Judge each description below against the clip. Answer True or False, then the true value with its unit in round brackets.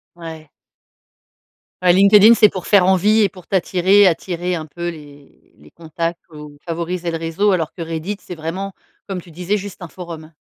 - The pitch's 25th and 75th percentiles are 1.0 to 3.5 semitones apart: True (2.8 semitones)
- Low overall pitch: False (175 Hz)